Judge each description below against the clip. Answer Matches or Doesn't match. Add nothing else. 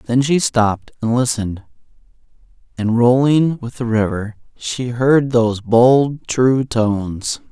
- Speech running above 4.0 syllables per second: Doesn't match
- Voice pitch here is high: Doesn't match